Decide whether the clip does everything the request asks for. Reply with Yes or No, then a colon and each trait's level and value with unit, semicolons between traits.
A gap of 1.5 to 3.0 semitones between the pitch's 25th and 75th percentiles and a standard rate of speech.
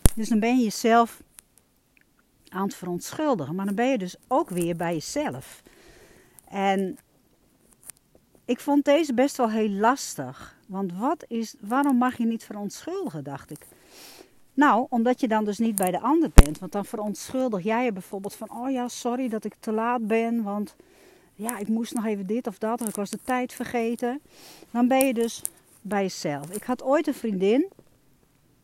No: average, 3.7 semitones; average, 180 wpm